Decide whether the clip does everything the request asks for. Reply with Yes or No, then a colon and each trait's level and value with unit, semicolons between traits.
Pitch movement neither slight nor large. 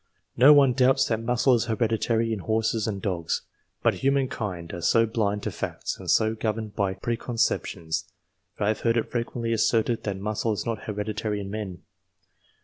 No: narrow, 2.2 semitones